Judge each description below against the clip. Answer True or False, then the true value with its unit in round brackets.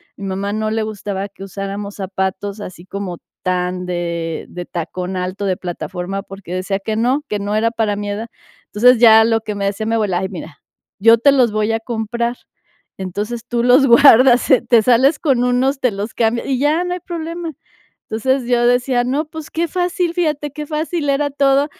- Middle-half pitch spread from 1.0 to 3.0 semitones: False (5.1 semitones)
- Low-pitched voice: False (225 Hz)